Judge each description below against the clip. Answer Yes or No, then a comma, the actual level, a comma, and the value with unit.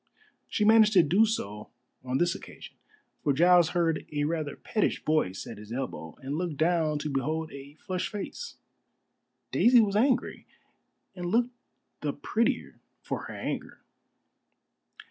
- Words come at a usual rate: Yes, average, 145 wpm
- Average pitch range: No, wide, 6.2 semitones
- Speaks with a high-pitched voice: No, medium, 165 Hz